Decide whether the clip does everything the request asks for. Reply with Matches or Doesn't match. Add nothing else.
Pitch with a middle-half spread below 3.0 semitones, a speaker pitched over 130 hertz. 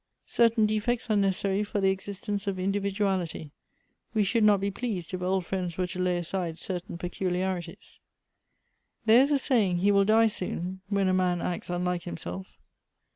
Matches